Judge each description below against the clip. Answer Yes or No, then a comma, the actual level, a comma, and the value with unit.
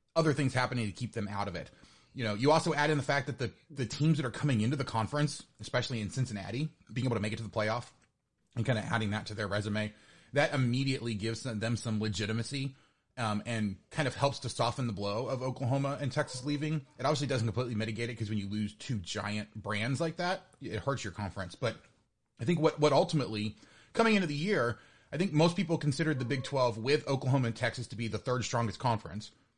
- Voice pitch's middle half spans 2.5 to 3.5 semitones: No, average, 4.8 semitones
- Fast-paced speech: Yes, fast, 230 wpm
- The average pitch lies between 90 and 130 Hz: Yes, low, 125 Hz